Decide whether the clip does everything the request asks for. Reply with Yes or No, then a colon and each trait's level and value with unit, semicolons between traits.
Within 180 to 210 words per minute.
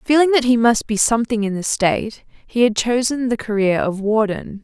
Yes: fast, 205 wpm